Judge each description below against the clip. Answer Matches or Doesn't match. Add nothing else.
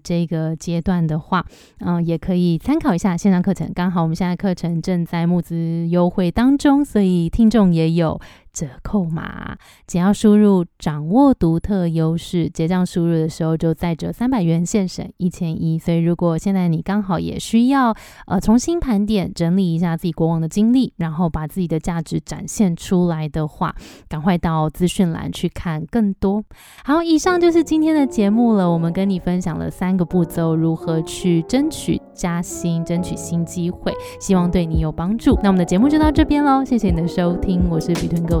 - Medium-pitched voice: Matches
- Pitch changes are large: Doesn't match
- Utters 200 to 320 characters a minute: Matches